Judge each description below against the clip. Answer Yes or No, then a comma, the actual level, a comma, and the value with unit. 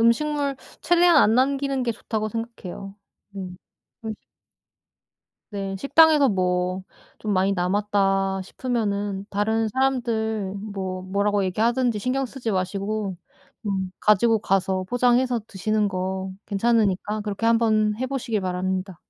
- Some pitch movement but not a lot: Yes, average, 3.6 semitones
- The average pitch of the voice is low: No, high, 210 Hz